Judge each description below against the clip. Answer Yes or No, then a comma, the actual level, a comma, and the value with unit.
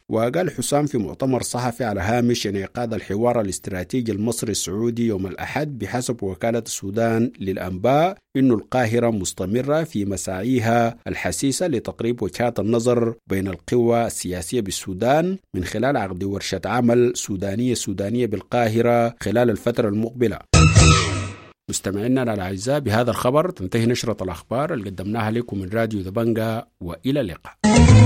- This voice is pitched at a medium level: No, low, 115 Hz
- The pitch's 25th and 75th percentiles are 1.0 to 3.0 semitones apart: No, average, 3.7 semitones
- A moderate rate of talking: No, slow, 120 wpm